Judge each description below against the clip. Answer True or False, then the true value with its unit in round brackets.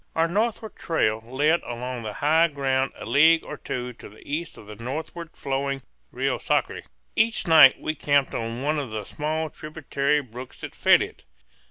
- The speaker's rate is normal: True (180 wpm)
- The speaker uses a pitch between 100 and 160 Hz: True (140 Hz)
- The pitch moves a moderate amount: True (4.0 semitones)